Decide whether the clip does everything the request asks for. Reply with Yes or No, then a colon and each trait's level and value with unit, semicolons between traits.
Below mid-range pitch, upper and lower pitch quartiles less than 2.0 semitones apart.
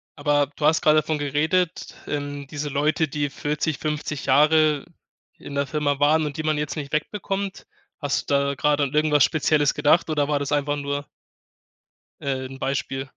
No: medium, 145 Hz; narrow, 1.4 semitones